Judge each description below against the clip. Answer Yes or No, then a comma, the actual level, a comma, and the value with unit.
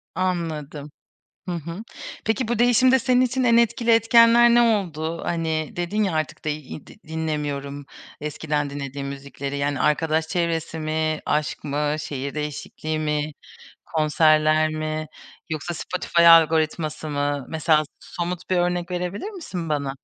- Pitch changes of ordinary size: Yes, average, 3.1 semitones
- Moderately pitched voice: Yes, medium, 155 Hz